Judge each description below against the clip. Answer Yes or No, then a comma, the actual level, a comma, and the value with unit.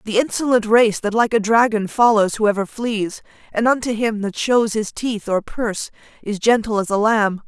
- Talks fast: No, average, 195 wpm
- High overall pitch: Yes, high, 220 Hz